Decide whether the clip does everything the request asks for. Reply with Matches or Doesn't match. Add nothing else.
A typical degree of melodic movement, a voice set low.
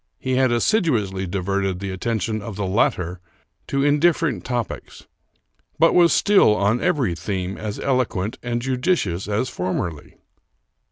Doesn't match